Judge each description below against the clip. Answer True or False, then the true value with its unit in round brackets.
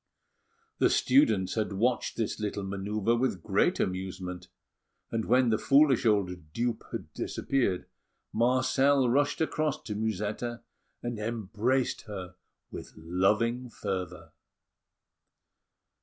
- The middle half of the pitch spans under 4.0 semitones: False (4.5 semitones)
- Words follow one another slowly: True (110 wpm)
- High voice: False (110 Hz)